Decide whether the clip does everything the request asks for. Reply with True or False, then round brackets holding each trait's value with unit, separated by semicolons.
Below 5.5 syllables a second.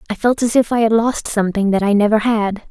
False (6.2 syllables/s)